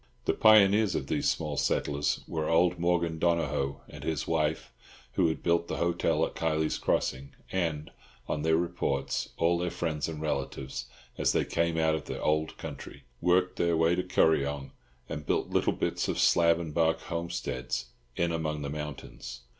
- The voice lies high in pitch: No, very low, 80 Hz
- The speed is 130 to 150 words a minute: No, average, 170 wpm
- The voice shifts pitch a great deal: No, narrow, 2.5 semitones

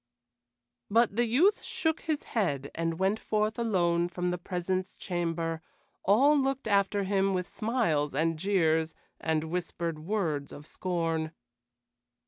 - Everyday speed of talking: No, slow, 130 wpm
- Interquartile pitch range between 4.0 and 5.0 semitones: Yes, average, 4.7 semitones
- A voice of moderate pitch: Yes, medium, 180 Hz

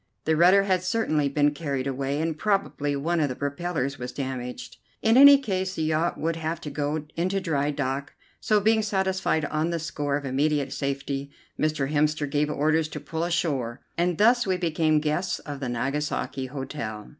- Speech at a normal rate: Yes, average, 180 wpm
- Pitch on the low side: No, medium, 150 Hz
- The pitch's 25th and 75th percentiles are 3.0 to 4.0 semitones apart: Yes, average, 3.6 semitones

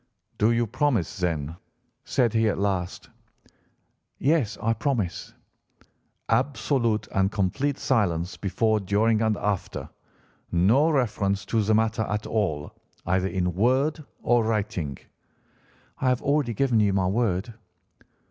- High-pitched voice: No, low, 110 Hz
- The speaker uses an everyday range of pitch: Yes, average, 3.9 semitones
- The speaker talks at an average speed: No, slow, 125 wpm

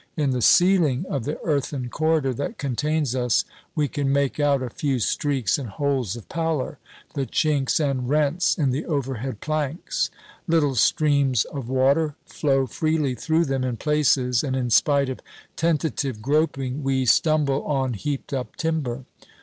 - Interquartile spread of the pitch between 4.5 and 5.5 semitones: No, average, 2.8 semitones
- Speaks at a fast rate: No, average, 160 wpm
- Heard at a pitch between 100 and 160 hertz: Yes, medium, 140 Hz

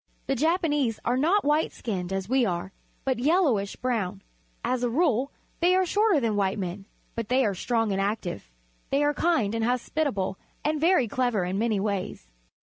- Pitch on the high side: Yes, high, 240 Hz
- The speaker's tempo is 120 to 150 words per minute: No, average, 180 wpm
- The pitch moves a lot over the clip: Yes, wide, 6.6 semitones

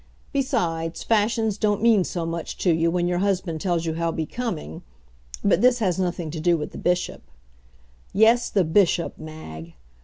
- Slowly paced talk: No, average, 165 wpm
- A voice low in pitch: No, medium, 175 Hz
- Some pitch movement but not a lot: Yes, average, 4.1 semitones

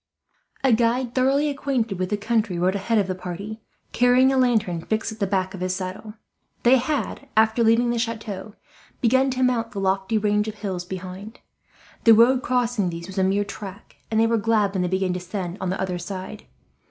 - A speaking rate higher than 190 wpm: Yes, fast, 205 wpm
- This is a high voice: Yes, high, 215 Hz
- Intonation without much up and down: No, average, 3.8 semitones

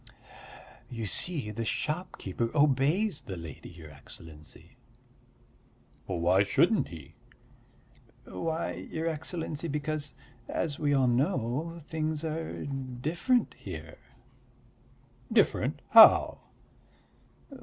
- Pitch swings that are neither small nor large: No, wide, 6.9 semitones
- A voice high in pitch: No, medium, 145 Hz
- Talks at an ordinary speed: No, slow, 90 wpm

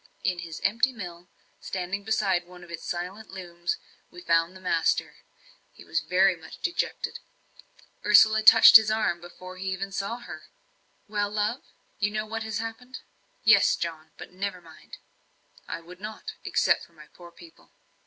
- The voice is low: No, high, 190 Hz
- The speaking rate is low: No, average, 165 wpm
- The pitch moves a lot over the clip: No, average, 3.7 semitones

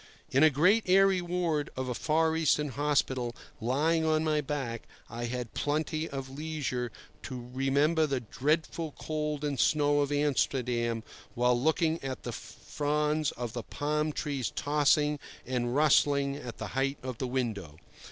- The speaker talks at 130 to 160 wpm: Yes, average, 150 wpm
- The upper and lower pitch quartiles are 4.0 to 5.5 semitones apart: No, average, 3.3 semitones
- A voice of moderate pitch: Yes, medium, 145 Hz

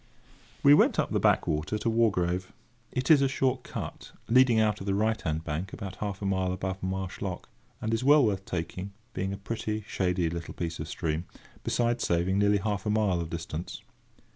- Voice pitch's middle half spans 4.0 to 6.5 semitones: No, average, 3.6 semitones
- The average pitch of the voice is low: Yes, very low, 95 Hz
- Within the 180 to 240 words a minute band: Yes, average, 195 wpm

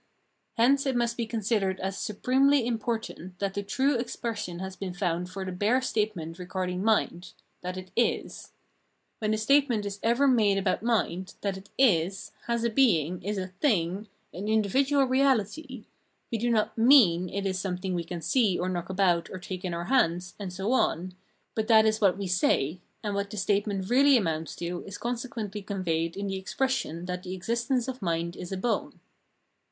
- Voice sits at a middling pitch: No, high, 200 Hz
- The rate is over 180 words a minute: Yes, average, 190 wpm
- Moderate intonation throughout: Yes, average, 4.4 semitones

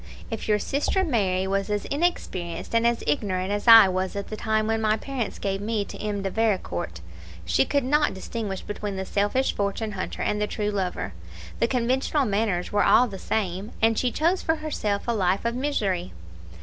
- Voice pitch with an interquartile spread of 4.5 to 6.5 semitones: No, average, 3.4 semitones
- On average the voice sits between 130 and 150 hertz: No, high, 210 Hz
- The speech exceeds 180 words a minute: Yes, average, 195 wpm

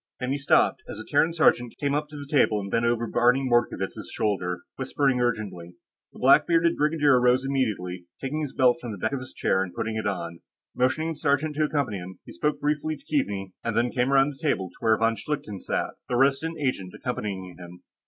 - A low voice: Yes, low, 125 Hz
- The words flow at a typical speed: No, fast, 220 wpm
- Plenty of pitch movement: Yes, wide, 5.7 semitones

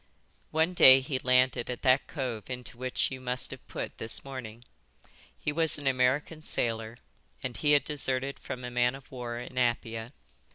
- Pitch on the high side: No, low, 130 Hz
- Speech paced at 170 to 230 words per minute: Yes, average, 175 wpm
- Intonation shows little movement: Yes, narrow, 2.0 semitones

